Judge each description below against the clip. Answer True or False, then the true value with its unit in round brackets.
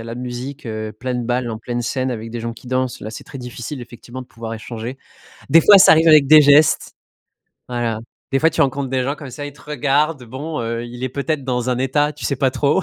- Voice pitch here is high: False (130 Hz)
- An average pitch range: True (3.2 semitones)